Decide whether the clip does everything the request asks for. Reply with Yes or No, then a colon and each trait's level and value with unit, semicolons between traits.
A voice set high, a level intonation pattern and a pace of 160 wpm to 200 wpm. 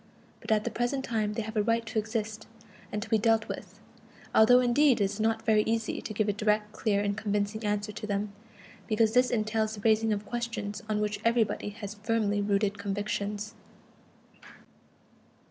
Yes: high, 215 Hz; narrow, 1.5 semitones; average, 180 wpm